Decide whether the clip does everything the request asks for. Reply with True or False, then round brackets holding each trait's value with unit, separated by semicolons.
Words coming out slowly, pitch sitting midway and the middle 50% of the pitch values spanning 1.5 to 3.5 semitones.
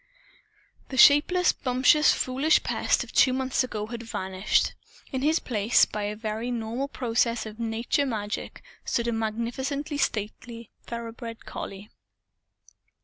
False (130 wpm; 235 Hz; 3.1 semitones)